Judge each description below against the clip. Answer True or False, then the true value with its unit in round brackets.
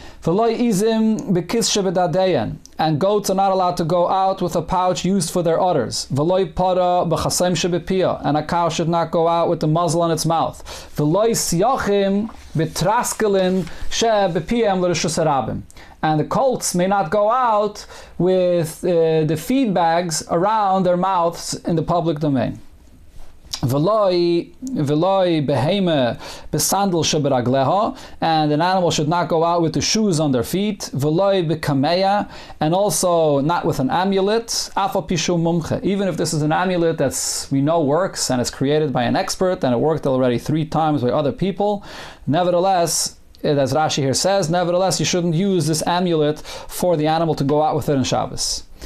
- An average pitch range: True (3.6 semitones)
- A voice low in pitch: False (170 Hz)